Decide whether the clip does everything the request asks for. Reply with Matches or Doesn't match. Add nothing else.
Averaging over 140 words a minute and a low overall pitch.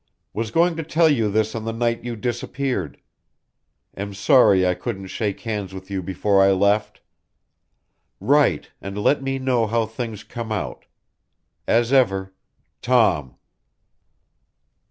Doesn't match